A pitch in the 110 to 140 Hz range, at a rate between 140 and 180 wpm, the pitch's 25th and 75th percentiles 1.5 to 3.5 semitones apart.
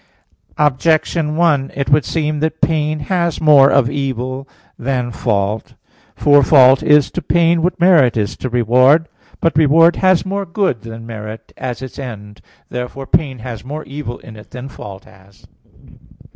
No: low, 135 Hz; average, 160 wpm; average, 4.4 semitones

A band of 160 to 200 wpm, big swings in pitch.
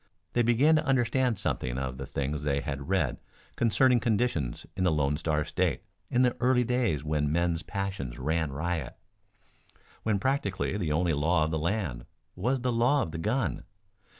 Yes: average, 175 wpm; wide, 8.1 semitones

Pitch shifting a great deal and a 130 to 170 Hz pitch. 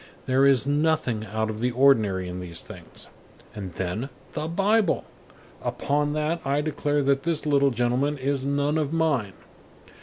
No: average, 4.7 semitones; medium, 140 Hz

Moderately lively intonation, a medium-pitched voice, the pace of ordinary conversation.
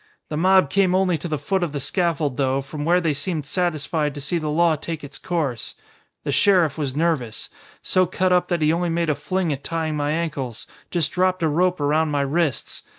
No: average, 3.3 semitones; medium, 160 Hz; fast, 215 wpm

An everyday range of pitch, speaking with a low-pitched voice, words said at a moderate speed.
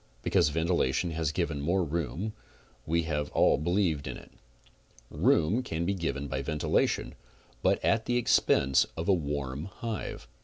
Yes: average, 4.3 semitones; very low, 80 Hz; average, 150 wpm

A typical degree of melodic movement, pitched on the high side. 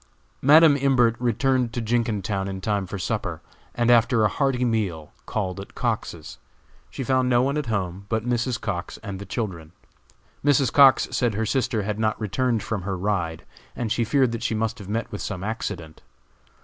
No: average, 3.8 semitones; low, 110 Hz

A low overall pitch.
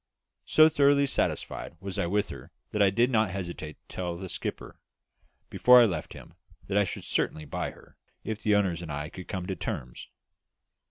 Yes: very low, 95 Hz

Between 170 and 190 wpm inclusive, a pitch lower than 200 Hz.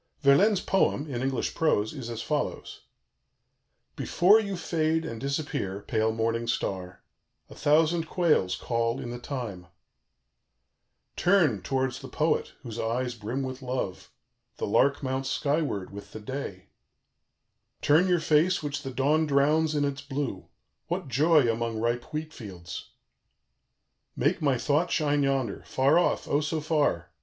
No: average, 145 wpm; low, 135 Hz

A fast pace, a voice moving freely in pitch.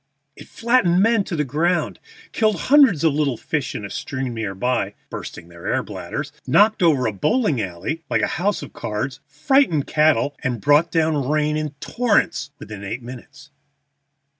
No: average, 170 wpm; wide, 6.0 semitones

